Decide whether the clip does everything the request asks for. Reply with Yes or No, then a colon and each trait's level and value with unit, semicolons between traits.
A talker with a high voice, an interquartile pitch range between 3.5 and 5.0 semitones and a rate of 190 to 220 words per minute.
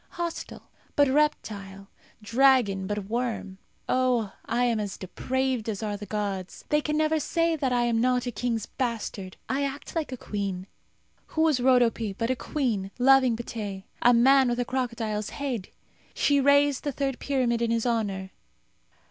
No: high, 240 Hz; average, 4.3 semitones; average, 165 wpm